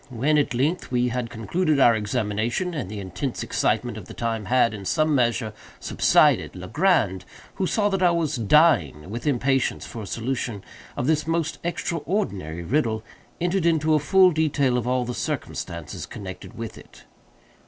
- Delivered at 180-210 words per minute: No, average, 165 wpm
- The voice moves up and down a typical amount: No, wide, 6.3 semitones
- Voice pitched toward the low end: Yes, low, 125 Hz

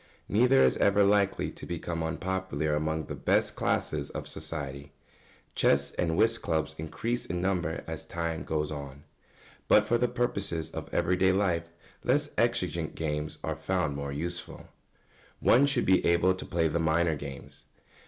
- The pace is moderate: Yes, average, 160 wpm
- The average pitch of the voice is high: No, very low, 85 Hz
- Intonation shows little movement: No, average, 3.5 semitones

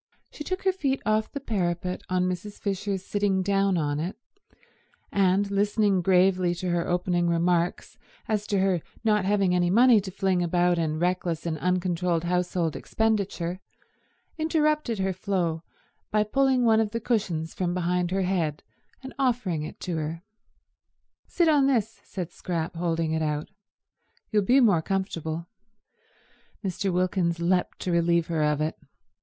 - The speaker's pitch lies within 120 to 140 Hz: No, medium, 185 Hz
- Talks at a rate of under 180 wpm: Yes, average, 155 wpm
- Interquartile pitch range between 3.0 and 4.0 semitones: Yes, average, 3.4 semitones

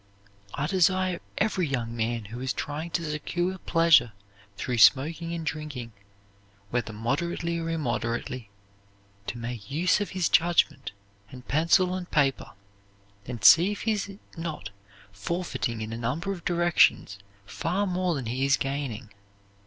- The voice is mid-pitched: Yes, medium, 150 Hz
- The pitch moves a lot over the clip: Yes, wide, 6.3 semitones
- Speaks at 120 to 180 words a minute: Yes, average, 145 wpm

